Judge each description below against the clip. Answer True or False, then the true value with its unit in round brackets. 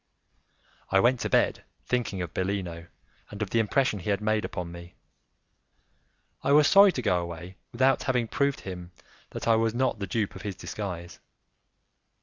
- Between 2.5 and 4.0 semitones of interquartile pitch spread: False (5.0 semitones)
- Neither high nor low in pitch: False (105 Hz)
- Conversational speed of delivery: True (175 wpm)